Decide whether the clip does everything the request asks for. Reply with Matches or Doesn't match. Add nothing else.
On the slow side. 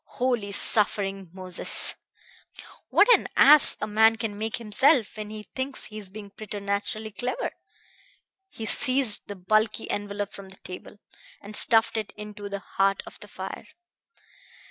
Doesn't match